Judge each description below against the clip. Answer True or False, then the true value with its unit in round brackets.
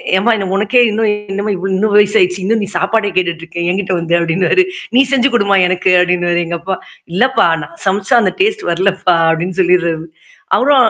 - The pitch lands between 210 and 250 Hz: False (190 Hz)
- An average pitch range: True (3.3 semitones)